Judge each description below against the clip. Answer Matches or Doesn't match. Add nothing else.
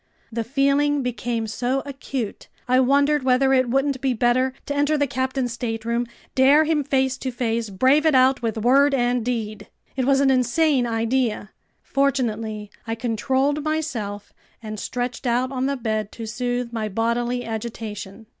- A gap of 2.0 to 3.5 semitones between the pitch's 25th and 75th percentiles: Matches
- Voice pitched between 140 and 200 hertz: Doesn't match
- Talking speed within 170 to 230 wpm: Doesn't match